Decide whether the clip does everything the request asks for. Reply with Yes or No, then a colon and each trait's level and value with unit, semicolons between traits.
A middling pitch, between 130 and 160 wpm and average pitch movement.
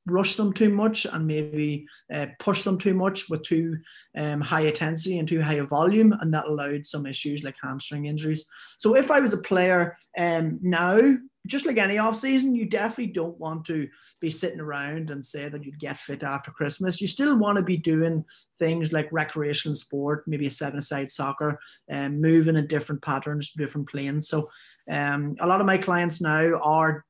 No: medium, 155 Hz; average, 200 wpm; average, 4.1 semitones